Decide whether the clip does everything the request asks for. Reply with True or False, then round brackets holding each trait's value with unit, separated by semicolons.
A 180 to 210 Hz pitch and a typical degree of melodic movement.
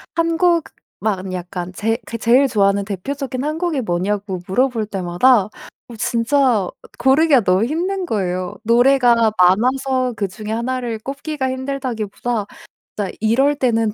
False (235 Hz; 5.0 semitones)